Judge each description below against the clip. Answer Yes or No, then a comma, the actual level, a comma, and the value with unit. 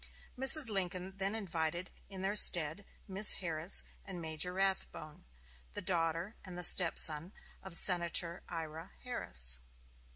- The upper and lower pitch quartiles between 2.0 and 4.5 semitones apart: Yes, average, 3.0 semitones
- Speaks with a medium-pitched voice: Yes, medium, 180 Hz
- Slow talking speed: Yes, slow, 125 wpm